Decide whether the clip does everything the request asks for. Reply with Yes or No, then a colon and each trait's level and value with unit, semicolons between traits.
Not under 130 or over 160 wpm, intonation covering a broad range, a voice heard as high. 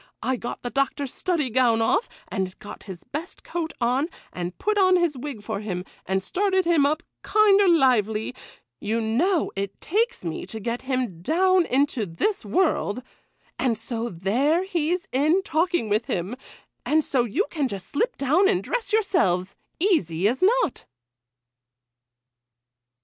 Yes: average, 145 wpm; wide, 8.8 semitones; very high, 270 Hz